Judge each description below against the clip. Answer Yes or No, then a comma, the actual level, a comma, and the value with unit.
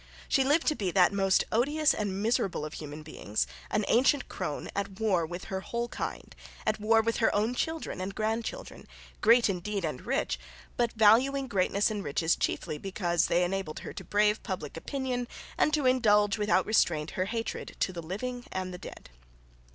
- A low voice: No, high, 210 Hz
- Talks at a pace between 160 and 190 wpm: Yes, average, 180 wpm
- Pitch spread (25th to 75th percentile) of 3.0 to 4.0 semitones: No, average, 4.5 semitones